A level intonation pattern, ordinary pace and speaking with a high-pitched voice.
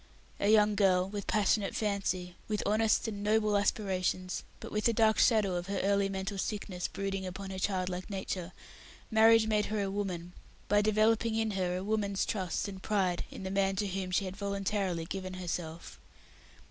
Yes: narrow, 2.2 semitones; average, 180 wpm; high, 195 Hz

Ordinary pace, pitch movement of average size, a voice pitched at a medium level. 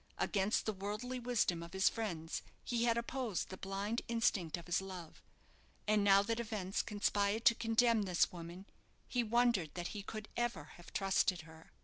No: average, 170 wpm; average, 4.1 semitones; high, 205 Hz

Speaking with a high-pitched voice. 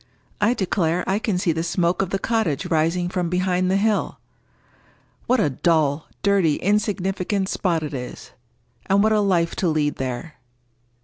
No: medium, 180 Hz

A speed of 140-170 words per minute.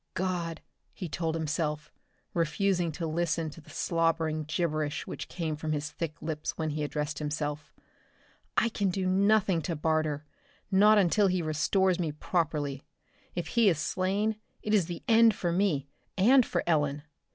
Yes: average, 160 wpm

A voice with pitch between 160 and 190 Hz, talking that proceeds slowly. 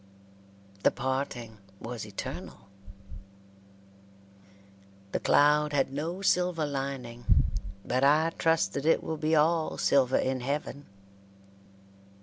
No: medium, 140 Hz; slow, 105 wpm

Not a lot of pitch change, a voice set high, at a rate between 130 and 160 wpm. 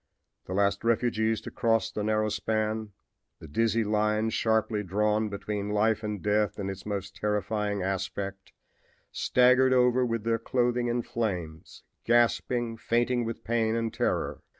No: narrow, 2.0 semitones; low, 110 Hz; average, 145 wpm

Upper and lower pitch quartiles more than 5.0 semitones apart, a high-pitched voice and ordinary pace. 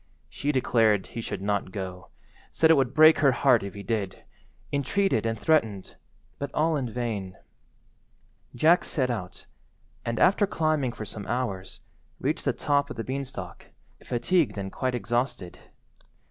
No: wide, 5.5 semitones; low, 120 Hz; average, 150 wpm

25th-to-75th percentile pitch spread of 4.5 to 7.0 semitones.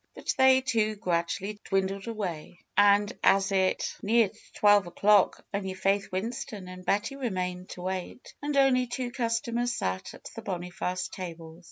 No: average, 3.9 semitones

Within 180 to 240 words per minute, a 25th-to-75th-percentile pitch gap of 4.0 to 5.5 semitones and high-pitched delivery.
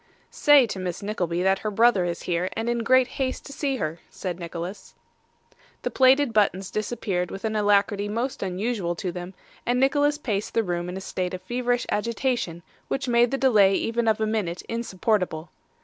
Yes: average, 185 wpm; average, 4.9 semitones; high, 210 Hz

